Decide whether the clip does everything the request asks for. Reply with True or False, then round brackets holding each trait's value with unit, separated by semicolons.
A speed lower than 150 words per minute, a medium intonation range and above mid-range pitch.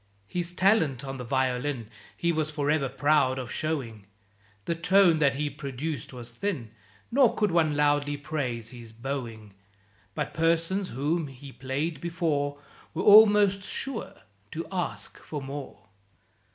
False (140 wpm; 4.3 semitones; 145 Hz)